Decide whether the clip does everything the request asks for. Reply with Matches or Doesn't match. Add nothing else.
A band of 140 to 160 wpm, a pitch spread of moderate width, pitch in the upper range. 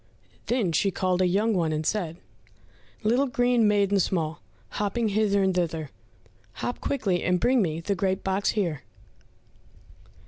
Matches